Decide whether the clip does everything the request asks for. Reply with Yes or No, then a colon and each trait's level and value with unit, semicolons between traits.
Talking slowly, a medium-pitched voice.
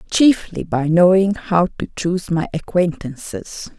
Yes: slow, 125 wpm; medium, 175 Hz